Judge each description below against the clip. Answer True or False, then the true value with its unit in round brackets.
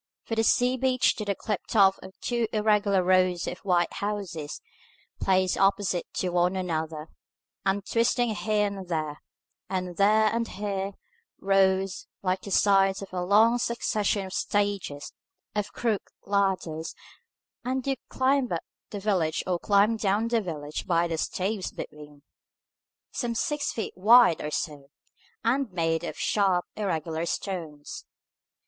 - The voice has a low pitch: False (195 Hz)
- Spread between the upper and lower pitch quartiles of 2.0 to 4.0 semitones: True (3.4 semitones)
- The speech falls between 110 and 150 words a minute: True (140 wpm)